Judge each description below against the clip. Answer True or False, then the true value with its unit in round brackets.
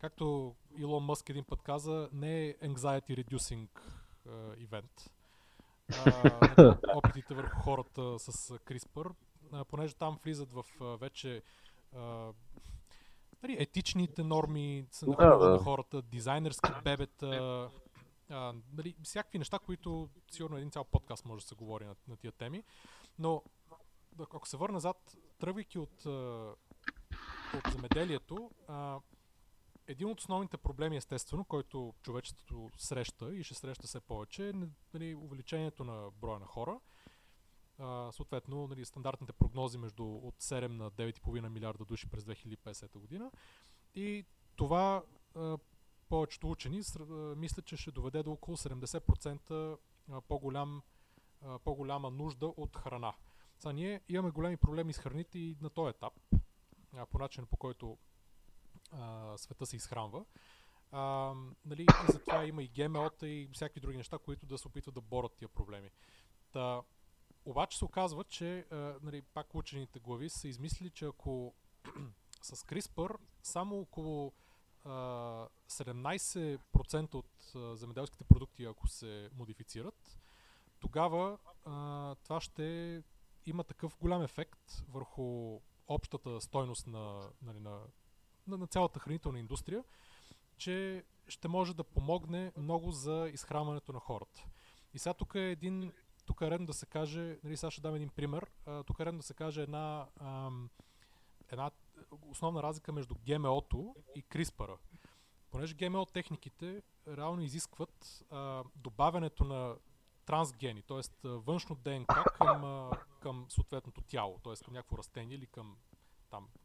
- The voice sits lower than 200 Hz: True (140 Hz)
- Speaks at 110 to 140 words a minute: True (135 wpm)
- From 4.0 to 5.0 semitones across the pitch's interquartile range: True (4.3 semitones)